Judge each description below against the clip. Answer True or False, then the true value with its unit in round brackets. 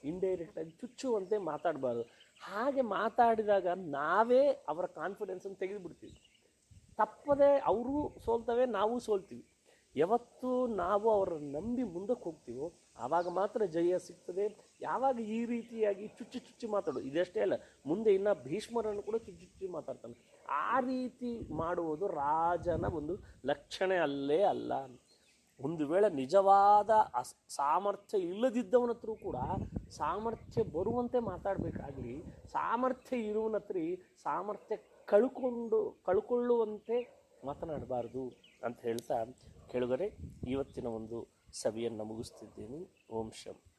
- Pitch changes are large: True (6.5 semitones)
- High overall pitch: True (205 Hz)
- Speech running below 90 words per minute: False (100 wpm)